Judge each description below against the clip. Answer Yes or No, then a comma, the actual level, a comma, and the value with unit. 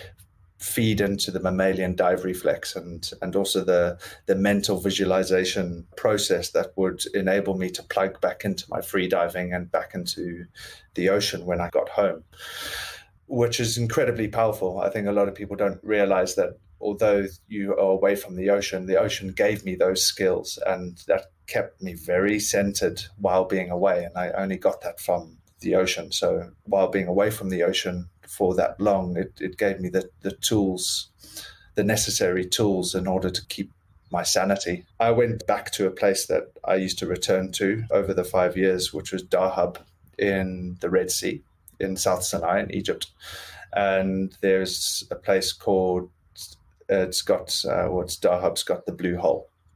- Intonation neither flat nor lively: No, narrow, 1.6 semitones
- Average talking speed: Yes, average, 175 wpm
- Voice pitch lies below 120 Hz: Yes, very low, 95 Hz